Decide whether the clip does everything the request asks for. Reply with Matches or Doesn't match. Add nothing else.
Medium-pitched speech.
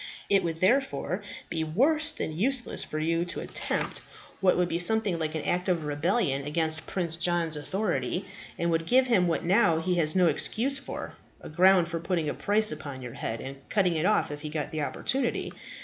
Matches